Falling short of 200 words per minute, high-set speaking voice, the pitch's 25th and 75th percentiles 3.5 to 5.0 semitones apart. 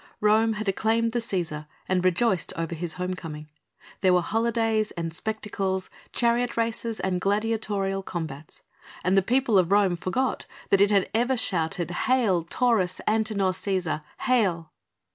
Yes: average, 145 wpm; high, 195 Hz; average, 3.9 semitones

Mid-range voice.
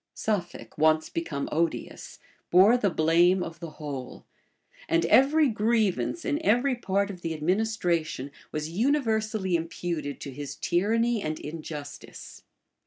Yes: medium, 175 Hz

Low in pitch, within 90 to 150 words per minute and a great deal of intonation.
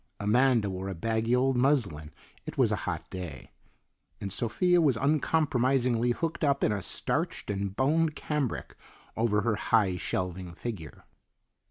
Yes: low, 115 Hz; average, 145 wpm; wide, 5.7 semitones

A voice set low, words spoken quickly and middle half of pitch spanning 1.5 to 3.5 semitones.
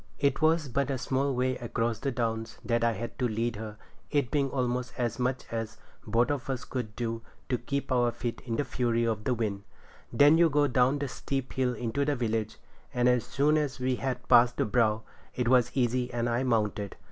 Yes: low, 125 Hz; fast, 215 wpm; narrow, 2.6 semitones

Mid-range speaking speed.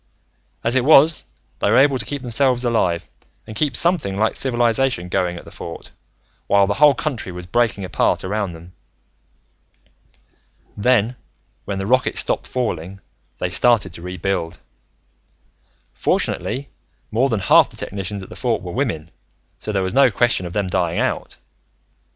Yes: average, 155 wpm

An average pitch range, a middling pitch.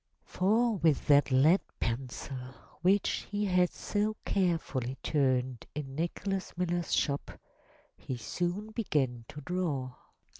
No: wide, 6.1 semitones; medium, 165 Hz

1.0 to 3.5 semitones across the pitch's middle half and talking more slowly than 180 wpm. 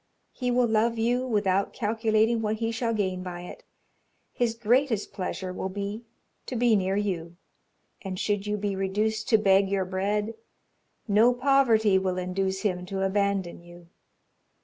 Yes: average, 2.9 semitones; average, 155 wpm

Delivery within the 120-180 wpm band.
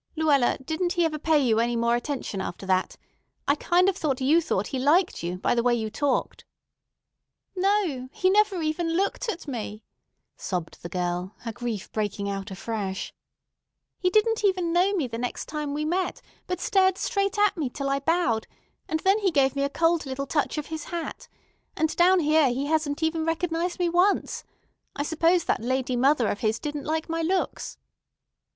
No: average, 190 wpm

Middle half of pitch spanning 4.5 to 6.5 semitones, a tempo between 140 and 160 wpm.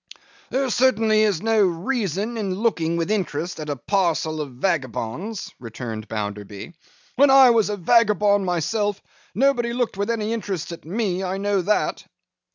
Yes: average, 5.3 semitones; average, 155 wpm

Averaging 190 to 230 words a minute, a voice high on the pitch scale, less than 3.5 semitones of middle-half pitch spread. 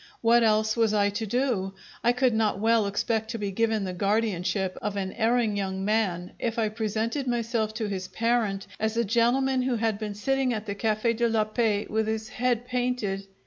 Yes: average, 200 wpm; high, 220 Hz; narrow, 2.4 semitones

